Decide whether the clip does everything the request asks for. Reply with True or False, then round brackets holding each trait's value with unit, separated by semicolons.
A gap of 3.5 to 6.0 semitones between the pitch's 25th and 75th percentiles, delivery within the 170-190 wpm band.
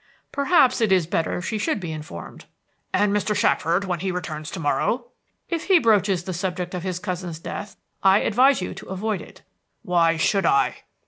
True (3.9 semitones; 185 wpm)